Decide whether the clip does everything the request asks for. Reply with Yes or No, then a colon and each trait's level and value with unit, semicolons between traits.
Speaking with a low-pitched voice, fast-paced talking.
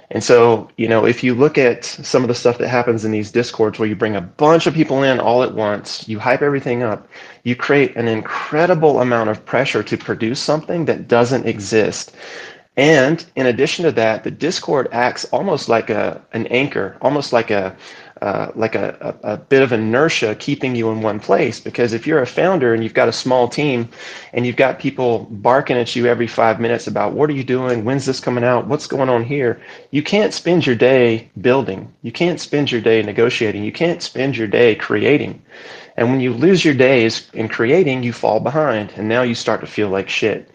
Yes: low, 120 Hz; fast, 215 wpm